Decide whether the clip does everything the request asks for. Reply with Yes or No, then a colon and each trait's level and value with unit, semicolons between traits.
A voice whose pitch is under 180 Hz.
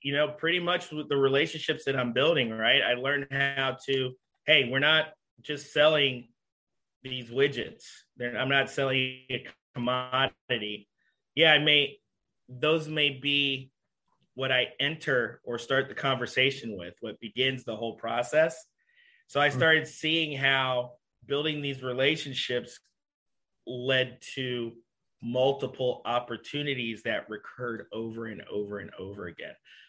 Yes: low, 135 Hz